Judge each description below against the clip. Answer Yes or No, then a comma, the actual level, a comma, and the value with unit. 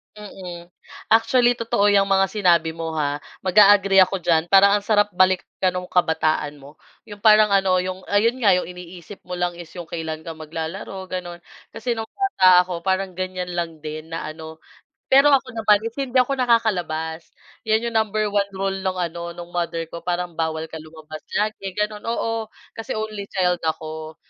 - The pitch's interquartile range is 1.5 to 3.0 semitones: No, average, 3.8 semitones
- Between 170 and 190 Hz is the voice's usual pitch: Yes, medium, 185 Hz